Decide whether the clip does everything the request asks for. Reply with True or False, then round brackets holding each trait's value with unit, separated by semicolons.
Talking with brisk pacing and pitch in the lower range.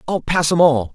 False (255 wpm; 155 Hz)